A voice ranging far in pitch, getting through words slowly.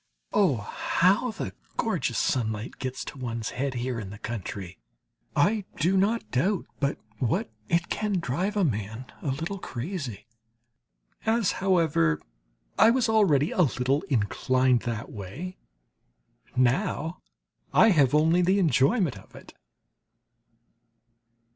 Yes: wide, 7.7 semitones; slow, 125 wpm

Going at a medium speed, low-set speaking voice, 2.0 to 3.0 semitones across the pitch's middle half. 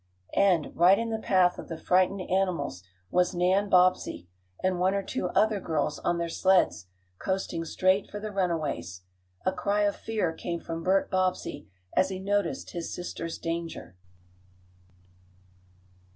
No: average, 150 wpm; medium, 185 Hz; narrow, 2.6 semitones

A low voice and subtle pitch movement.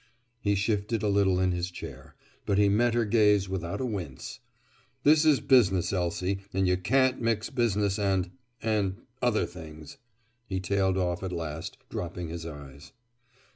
No: very low, 95 Hz; average, 3.6 semitones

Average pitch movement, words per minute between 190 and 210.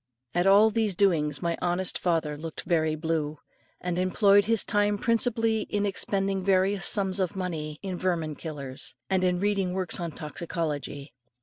No: average, 3.6 semitones; average, 160 wpm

